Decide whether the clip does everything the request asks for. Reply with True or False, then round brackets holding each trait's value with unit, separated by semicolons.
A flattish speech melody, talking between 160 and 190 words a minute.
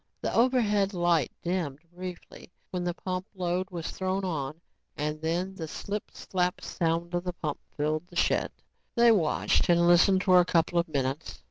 True (2.3 semitones; 170 wpm)